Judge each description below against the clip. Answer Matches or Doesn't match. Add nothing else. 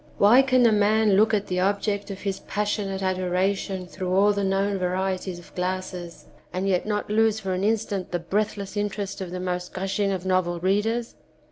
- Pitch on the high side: Matches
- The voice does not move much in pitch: Matches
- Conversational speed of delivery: Matches